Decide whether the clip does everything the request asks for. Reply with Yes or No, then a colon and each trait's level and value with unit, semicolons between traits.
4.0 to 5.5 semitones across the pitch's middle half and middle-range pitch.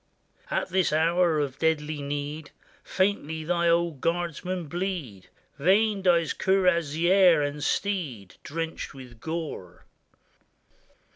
No: average, 3.6 semitones; medium, 165 Hz